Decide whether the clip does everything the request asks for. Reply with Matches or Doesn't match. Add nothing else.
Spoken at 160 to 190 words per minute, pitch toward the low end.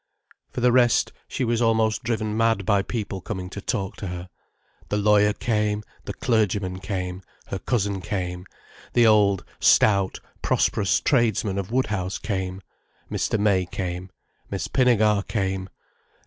Doesn't match